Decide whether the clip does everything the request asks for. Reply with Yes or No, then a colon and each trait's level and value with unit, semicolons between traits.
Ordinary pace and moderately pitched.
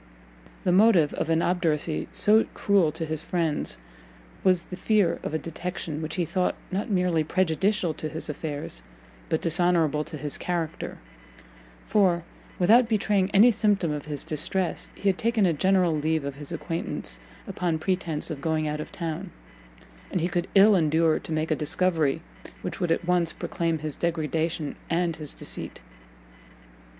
Yes: average, 160 wpm; medium, 170 Hz